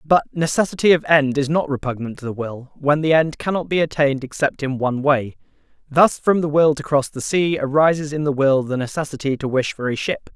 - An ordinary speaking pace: No, fast, 225 wpm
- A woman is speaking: No, male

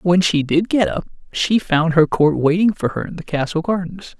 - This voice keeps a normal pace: No, fast, 230 wpm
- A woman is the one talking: No, male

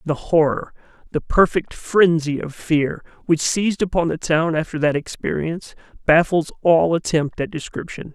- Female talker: No, male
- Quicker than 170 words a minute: No, average, 145 wpm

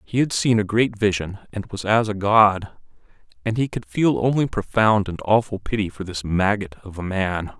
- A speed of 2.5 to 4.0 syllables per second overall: No, 4.9 syllables/s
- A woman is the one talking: No, male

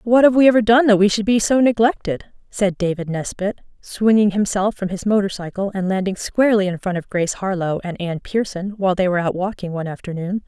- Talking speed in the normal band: No, fast, 210 wpm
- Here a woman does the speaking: Yes, female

